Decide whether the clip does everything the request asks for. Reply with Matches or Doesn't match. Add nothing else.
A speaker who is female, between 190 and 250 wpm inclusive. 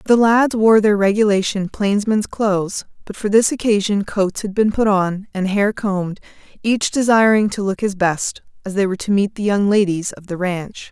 Matches